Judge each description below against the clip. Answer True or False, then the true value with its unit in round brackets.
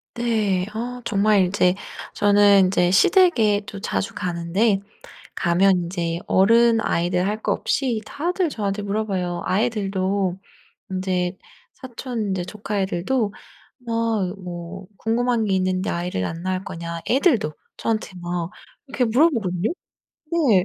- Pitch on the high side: True (200 Hz)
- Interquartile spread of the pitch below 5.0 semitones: True (3.9 semitones)